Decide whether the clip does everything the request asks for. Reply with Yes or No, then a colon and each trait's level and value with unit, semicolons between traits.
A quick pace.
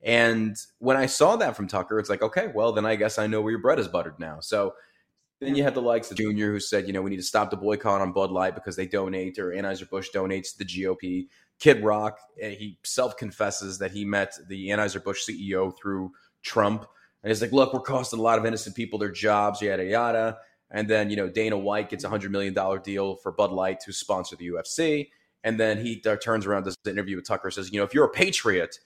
Yes: fast, 245 wpm